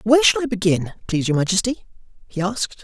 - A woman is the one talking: No, male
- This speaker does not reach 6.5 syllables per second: No, 6.9 syllables/s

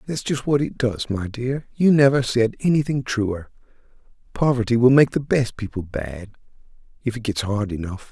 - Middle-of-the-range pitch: No, low, 120 Hz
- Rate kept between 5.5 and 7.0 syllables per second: No, 4.9 syllables/s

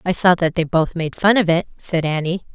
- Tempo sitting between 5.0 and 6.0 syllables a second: Yes, 5.2 syllables/s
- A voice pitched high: No, medium, 170 Hz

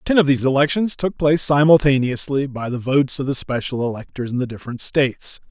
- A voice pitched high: No, low, 135 Hz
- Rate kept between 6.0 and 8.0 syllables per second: Yes, 6.2 syllables/s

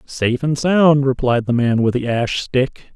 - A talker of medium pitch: No, low, 130 Hz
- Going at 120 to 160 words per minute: No, fast, 205 wpm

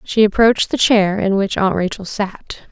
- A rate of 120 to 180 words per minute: No, average, 200 wpm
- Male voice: No, female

